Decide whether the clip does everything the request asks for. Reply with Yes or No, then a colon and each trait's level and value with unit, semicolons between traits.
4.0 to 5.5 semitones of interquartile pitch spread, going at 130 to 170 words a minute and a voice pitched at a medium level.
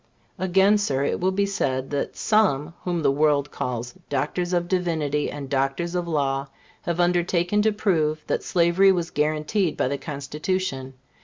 Yes: average, 4.4 semitones; average, 160 wpm; medium, 165 Hz